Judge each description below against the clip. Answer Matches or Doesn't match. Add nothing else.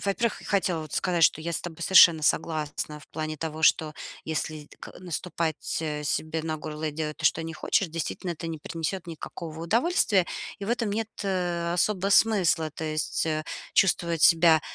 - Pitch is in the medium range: Matches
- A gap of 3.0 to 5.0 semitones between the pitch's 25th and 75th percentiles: Doesn't match